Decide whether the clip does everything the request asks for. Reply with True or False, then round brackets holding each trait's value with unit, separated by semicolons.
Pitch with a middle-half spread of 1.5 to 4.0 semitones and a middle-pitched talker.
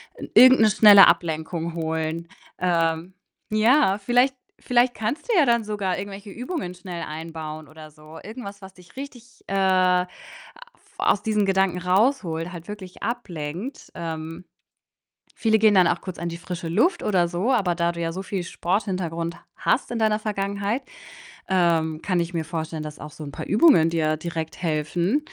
False (4.4 semitones; 180 Hz)